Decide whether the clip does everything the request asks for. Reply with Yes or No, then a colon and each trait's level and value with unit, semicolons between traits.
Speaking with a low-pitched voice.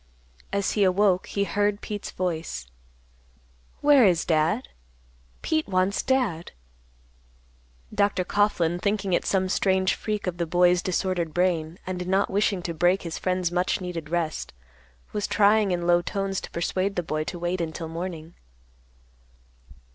No: medium, 185 Hz